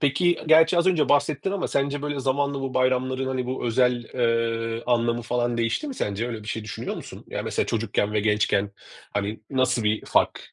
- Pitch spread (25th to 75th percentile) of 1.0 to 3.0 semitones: No, average, 3.5 semitones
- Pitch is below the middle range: Yes, low, 125 Hz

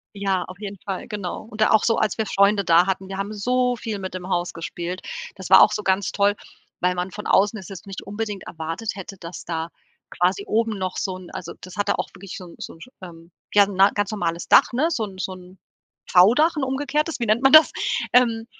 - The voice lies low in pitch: No, high, 195 Hz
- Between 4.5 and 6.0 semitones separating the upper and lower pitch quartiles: No, average, 2.9 semitones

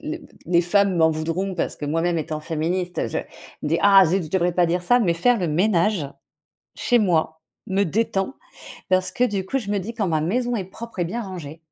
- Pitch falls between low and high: Yes, medium, 180 Hz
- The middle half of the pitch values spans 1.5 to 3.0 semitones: No, average, 3.7 semitones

